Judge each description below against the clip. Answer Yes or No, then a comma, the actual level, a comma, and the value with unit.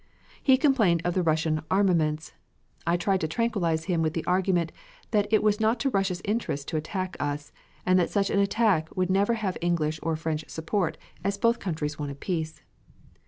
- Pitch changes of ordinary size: Yes, average, 4.2 semitones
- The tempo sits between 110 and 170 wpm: No, average, 185 wpm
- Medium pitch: Yes, medium, 180 Hz